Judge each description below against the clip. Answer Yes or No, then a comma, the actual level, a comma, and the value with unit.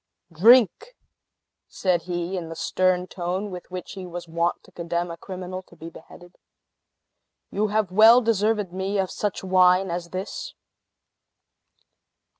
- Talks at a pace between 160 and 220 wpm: No, average, 140 wpm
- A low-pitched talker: No, medium, 185 Hz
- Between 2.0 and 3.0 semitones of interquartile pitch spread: Yes, narrow, 2.4 semitones